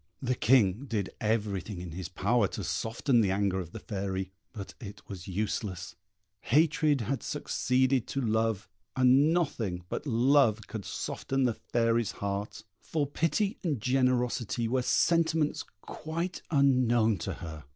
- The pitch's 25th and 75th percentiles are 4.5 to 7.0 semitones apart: Yes, average, 5.2 semitones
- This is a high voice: No, low, 115 Hz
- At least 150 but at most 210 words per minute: No, average, 140 wpm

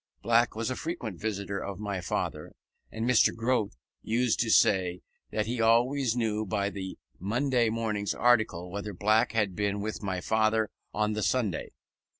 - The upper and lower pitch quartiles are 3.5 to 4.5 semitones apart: No, narrow, 2.4 semitones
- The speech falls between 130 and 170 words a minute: Yes, average, 160 wpm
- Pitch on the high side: No, low, 110 Hz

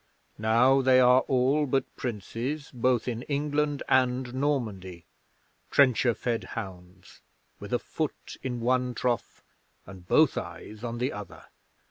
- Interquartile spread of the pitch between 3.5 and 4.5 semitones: No, average, 3.1 semitones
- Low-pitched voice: Yes, low, 125 Hz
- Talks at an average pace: No, slow, 130 wpm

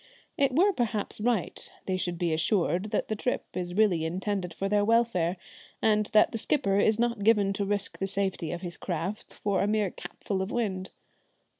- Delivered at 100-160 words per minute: No, average, 190 wpm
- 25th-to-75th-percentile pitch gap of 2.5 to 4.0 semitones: Yes, average, 2.9 semitones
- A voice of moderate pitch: No, high, 200 Hz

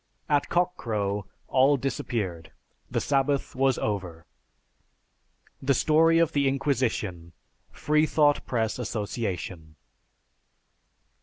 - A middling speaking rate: No, slow, 90 wpm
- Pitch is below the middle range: Yes, low, 130 Hz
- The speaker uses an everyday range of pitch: No, wide, 6.2 semitones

